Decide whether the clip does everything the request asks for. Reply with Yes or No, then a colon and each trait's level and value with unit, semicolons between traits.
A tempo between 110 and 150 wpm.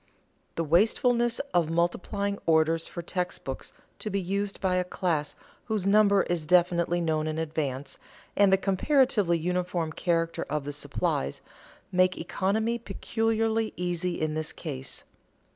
Yes: average, 140 wpm